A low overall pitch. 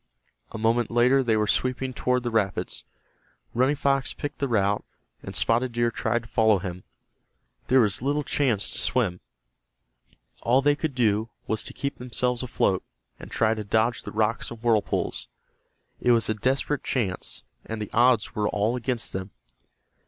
Yes: low, 115 Hz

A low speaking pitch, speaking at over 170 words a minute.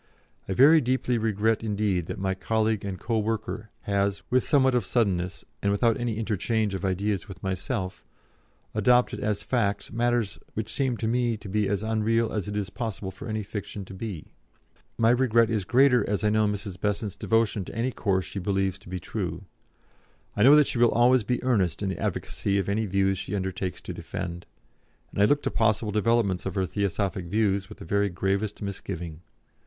Yes: low, 105 Hz; average, 195 wpm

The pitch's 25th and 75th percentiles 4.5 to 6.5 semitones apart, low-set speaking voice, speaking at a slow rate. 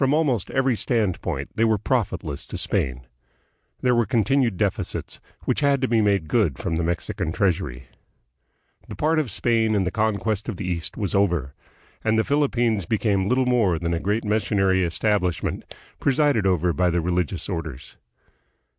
No: average, 5.2 semitones; low, 100 Hz; average, 170 wpm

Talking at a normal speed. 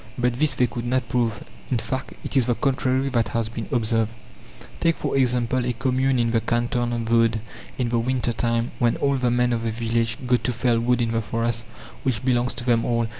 No: fast, 225 wpm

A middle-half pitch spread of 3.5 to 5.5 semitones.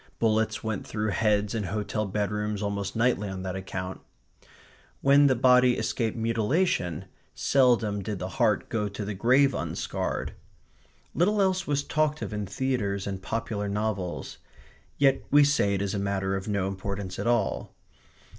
Yes: average, 3.9 semitones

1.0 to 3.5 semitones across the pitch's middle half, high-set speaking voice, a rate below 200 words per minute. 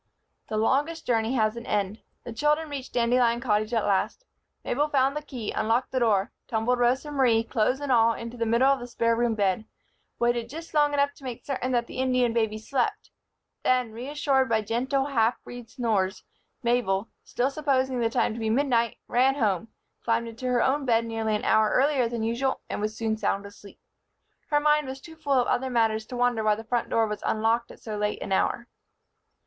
No: average, 2.9 semitones; high, 235 Hz; fast, 205 wpm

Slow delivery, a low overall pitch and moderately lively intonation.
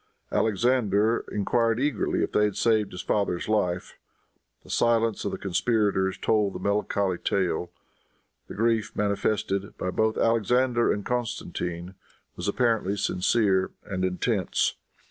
Yes: slow, 125 wpm; low, 105 Hz; average, 3.1 semitones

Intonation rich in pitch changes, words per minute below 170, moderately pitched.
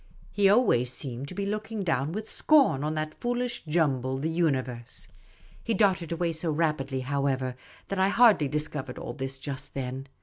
No: wide, 6.7 semitones; average, 175 wpm; medium, 155 Hz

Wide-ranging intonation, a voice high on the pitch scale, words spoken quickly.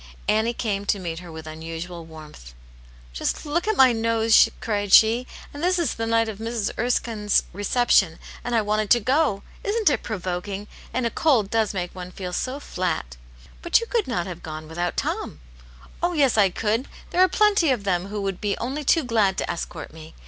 Yes: wide, 5.8 semitones; high, 210 Hz; fast, 220 wpm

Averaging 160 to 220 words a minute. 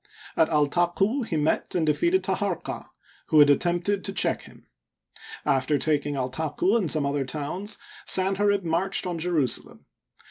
No: average, 140 wpm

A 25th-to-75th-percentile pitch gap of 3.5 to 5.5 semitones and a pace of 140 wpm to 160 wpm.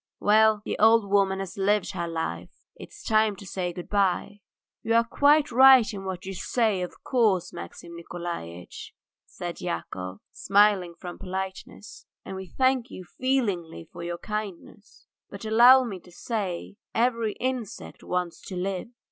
Yes: average, 3.9 semitones; average, 155 wpm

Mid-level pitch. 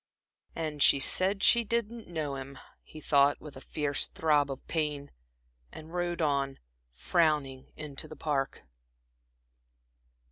Yes: medium, 150 Hz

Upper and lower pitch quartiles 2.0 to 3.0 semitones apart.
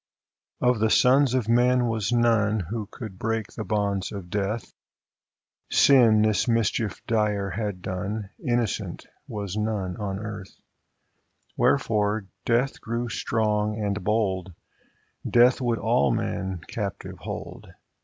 Yes: narrow, 2.6 semitones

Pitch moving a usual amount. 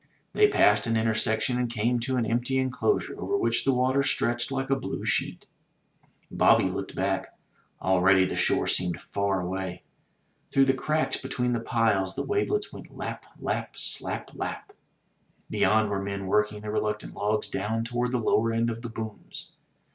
Yes: average, 3.5 semitones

